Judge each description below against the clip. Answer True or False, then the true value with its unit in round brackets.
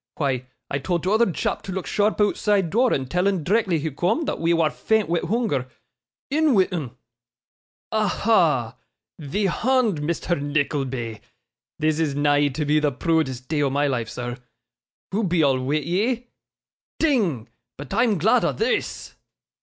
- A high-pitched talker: False (165 Hz)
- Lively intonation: True (6.5 semitones)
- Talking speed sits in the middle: True (160 wpm)